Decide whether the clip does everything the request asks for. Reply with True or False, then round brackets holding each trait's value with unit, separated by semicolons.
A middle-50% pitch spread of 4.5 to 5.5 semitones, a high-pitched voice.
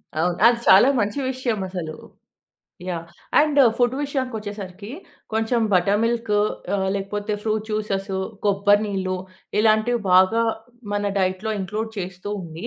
False (2.9 semitones; 205 Hz)